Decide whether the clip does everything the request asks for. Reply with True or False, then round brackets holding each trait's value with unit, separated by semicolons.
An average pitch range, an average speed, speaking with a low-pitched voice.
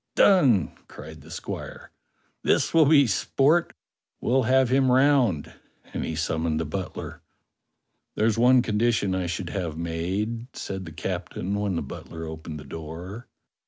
False (7.0 semitones; 145 wpm; 95 Hz)